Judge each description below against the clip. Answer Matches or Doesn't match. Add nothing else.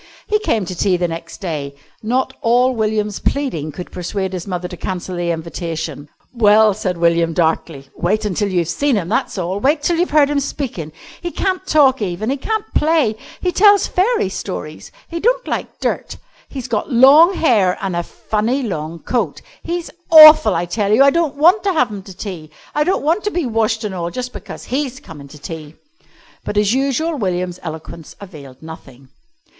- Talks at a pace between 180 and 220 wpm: Matches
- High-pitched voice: Matches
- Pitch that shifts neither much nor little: Doesn't match